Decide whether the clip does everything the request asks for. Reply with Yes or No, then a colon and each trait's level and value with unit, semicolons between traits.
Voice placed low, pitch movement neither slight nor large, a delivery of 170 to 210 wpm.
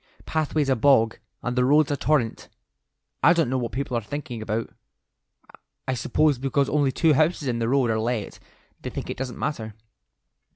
Yes: low, 130 Hz; average, 3.8 semitones; average, 180 wpm